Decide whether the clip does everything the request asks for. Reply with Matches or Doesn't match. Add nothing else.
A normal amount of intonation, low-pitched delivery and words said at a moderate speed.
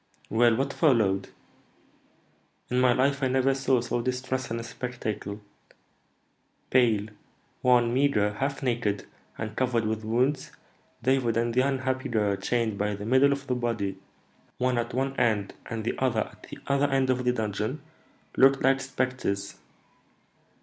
Matches